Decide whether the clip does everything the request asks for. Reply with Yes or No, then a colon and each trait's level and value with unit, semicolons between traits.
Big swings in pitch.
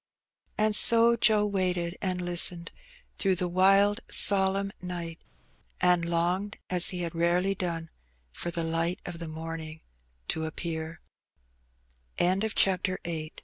No: narrow, 2.5 semitones